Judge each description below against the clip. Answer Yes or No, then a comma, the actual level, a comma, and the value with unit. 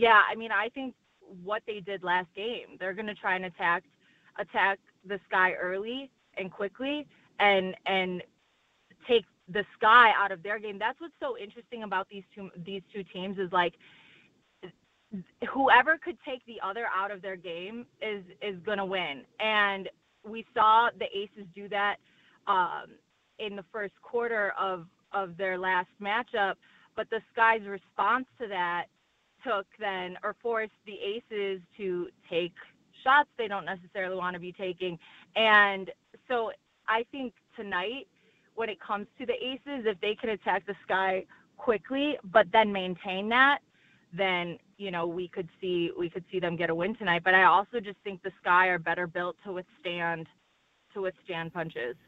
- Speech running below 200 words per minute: Yes, average, 165 wpm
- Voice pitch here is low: No, high, 200 Hz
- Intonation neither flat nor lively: Yes, average, 3.2 semitones